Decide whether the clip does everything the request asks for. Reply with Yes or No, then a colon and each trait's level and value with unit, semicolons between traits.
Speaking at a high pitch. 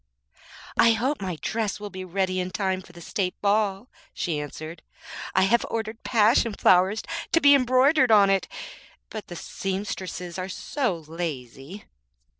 Yes: high, 195 Hz